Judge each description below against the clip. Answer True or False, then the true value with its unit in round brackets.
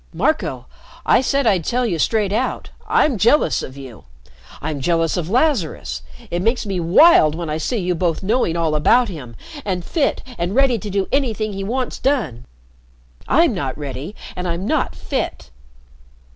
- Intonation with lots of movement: True (7.2 semitones)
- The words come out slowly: False (170 wpm)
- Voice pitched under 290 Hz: True (190 Hz)